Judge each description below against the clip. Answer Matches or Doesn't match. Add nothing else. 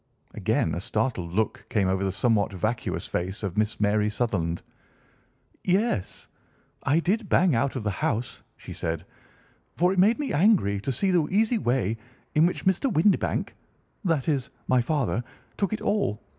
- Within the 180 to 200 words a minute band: Doesn't match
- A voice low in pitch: Matches